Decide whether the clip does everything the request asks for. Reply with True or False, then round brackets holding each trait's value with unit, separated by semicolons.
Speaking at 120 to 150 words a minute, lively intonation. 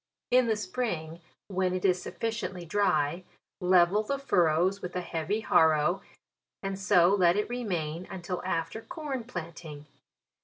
False (140 wpm; 3.7 semitones)